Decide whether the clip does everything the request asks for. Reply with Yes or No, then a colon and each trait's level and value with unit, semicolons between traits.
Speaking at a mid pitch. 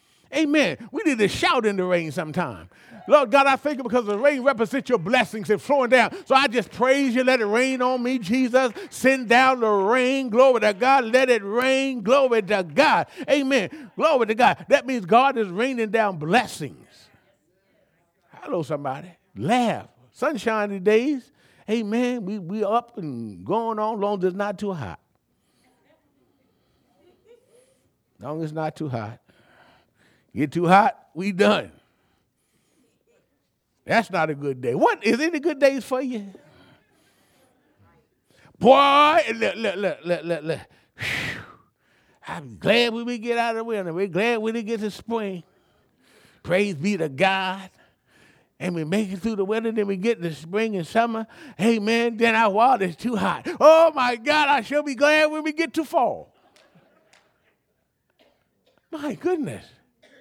No: high, 230 Hz